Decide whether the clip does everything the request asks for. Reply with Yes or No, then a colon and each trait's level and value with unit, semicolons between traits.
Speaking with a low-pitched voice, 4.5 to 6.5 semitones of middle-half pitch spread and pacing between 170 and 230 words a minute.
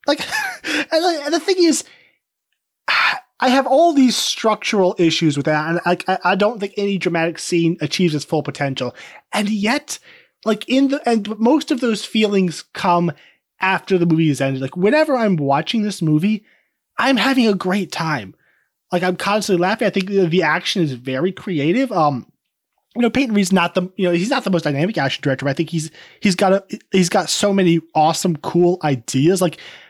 No: medium, 185 Hz; average, 4.8 semitones; average, 190 wpm